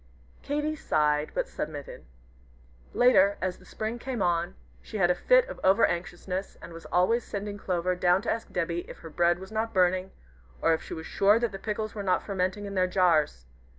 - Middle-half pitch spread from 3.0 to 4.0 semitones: Yes, average, 3.6 semitones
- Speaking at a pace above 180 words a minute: Yes, average, 200 wpm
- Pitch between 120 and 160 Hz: No, medium, 185 Hz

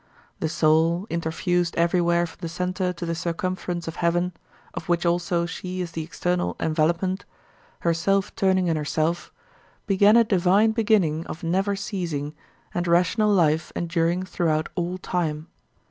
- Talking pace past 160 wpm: No, average, 145 wpm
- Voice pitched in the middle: Yes, medium, 175 Hz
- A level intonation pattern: Yes, narrow, 1.9 semitones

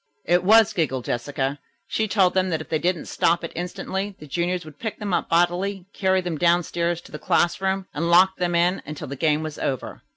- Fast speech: Yes, fast, 215 wpm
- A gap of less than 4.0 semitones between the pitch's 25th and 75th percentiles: Yes, average, 3.1 semitones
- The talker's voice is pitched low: No, medium, 175 Hz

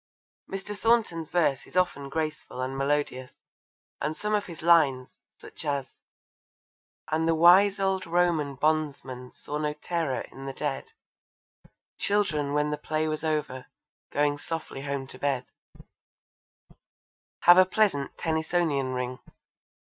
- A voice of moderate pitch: Yes, medium, 155 Hz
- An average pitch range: Yes, average, 3.9 semitones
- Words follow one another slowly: Yes, slow, 130 wpm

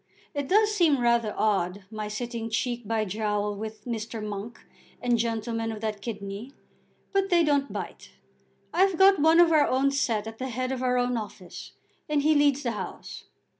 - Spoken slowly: No, average, 180 wpm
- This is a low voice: No, high, 235 Hz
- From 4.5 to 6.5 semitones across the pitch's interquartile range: Yes, average, 4.8 semitones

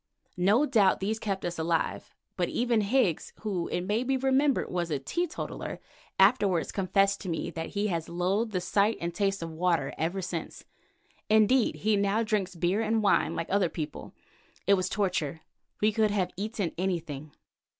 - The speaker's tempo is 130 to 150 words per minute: No, average, 170 wpm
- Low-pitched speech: No, high, 195 Hz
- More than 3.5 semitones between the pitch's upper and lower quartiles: Yes, average, 4.0 semitones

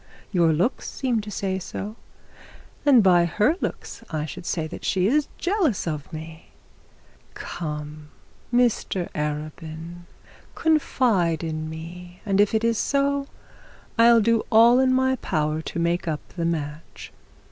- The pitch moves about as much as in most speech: No, wide, 6.5 semitones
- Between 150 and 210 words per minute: No, average, 140 wpm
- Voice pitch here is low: No, medium, 180 Hz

